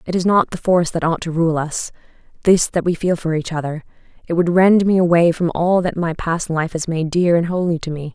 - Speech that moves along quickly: Yes, fast, 250 wpm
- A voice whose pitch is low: No, medium, 170 Hz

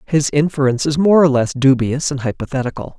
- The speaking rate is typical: Yes, average, 180 wpm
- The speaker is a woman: No, male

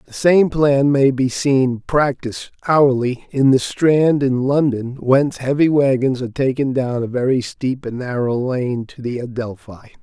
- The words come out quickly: No, average, 170 wpm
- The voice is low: Yes, low, 130 Hz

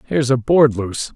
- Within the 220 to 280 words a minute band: No, fast, 205 wpm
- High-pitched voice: No, low, 125 Hz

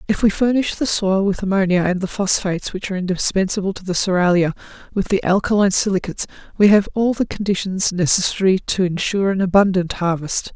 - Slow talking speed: No, average, 175 wpm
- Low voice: No, high, 190 Hz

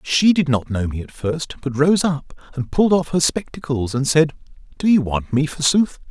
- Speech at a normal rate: No, fast, 215 wpm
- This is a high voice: No, medium, 145 Hz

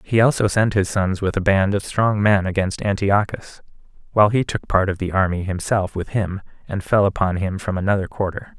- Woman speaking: No, male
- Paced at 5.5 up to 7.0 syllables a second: No, 5.3 syllables/s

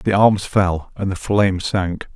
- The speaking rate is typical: Yes, average, 195 wpm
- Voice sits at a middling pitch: No, very low, 95 Hz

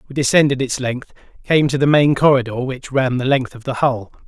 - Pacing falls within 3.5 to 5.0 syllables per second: No, 5.4 syllables/s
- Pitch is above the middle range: No, low, 130 Hz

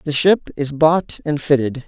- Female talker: No, male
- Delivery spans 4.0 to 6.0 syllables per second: Yes, 4.3 syllables/s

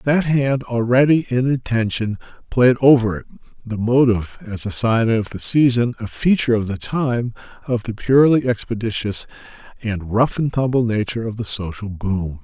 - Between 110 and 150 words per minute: No, average, 165 wpm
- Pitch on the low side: Yes, low, 115 Hz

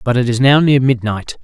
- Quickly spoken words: Yes, fast, 250 wpm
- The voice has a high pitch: No, low, 125 Hz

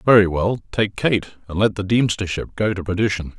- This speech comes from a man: Yes, male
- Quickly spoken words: No, average, 195 wpm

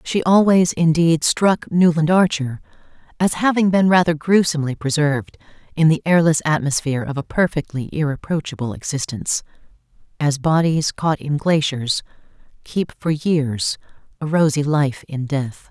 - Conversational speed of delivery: No, slow, 130 wpm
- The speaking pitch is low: No, medium, 155 Hz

